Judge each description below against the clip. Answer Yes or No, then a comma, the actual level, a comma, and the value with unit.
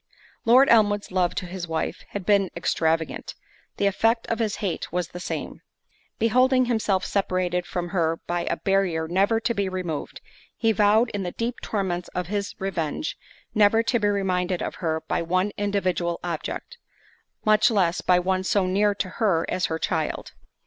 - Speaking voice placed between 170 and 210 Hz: Yes, high, 190 Hz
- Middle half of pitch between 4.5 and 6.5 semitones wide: No, average, 3.1 semitones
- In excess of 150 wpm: Yes, average, 170 wpm